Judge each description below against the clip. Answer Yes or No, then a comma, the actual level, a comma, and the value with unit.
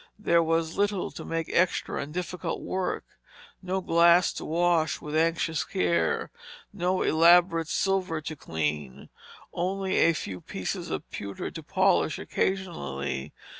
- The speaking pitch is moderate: Yes, medium, 165 Hz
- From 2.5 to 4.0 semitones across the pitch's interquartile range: Yes, average, 3.0 semitones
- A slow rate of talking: Yes, slow, 130 wpm